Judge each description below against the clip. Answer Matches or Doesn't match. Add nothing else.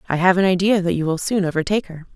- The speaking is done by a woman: Matches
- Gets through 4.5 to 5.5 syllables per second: Doesn't match